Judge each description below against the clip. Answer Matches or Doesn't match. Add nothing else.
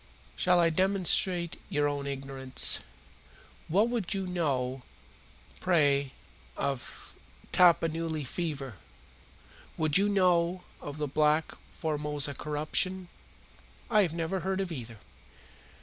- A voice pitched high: Doesn't match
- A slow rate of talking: Matches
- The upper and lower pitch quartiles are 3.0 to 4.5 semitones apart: Matches